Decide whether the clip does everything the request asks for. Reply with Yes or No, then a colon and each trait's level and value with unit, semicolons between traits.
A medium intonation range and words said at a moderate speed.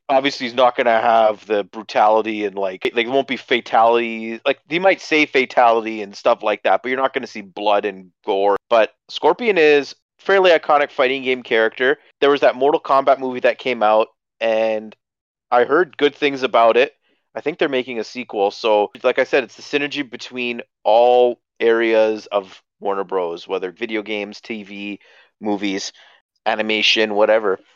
Yes: average, 3.7 semitones; average, 180 wpm